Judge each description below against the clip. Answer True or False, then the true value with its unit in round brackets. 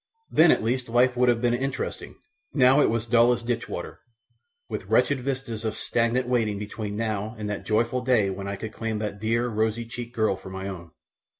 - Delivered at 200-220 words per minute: True (205 wpm)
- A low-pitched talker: True (115 Hz)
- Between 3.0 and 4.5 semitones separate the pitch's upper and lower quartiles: False (2.4 semitones)